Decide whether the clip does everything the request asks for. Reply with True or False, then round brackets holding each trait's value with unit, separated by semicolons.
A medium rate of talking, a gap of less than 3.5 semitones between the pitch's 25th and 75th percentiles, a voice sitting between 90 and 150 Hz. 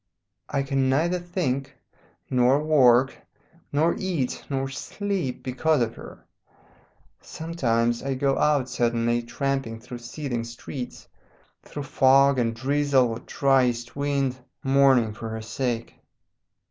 False (120 wpm; 2.9 semitones; 135 Hz)